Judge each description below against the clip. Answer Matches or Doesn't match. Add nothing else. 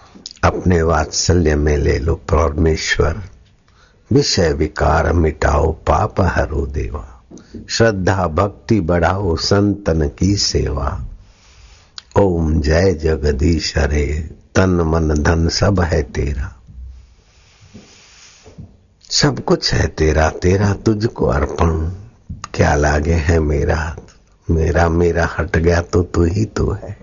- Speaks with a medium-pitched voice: Doesn't match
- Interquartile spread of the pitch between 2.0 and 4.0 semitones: Matches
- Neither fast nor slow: Doesn't match